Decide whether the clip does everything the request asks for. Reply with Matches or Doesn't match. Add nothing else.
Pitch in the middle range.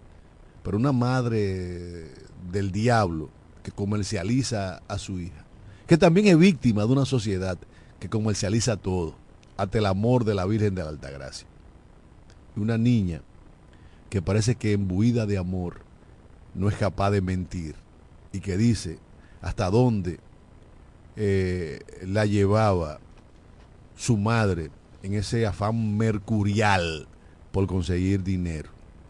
Doesn't match